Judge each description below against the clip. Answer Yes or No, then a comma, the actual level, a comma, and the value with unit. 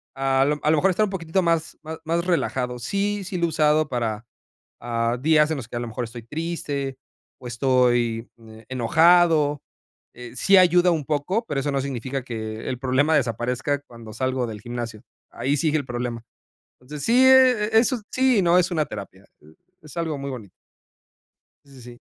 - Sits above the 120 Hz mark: Yes, medium, 140 Hz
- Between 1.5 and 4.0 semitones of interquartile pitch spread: No, wide, 5.6 semitones